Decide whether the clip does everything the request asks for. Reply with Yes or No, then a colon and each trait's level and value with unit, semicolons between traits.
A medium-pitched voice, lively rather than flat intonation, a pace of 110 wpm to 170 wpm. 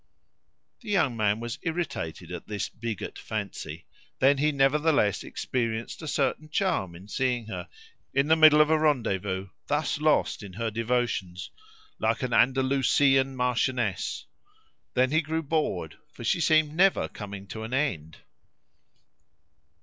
No: low, 130 Hz; wide, 5.9 semitones; average, 140 wpm